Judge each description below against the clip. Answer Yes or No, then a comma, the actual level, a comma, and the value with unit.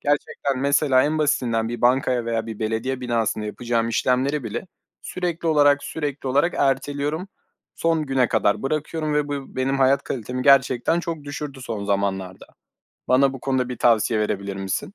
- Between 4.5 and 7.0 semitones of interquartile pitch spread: No, average, 3.8 semitones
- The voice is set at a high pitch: No, low, 130 Hz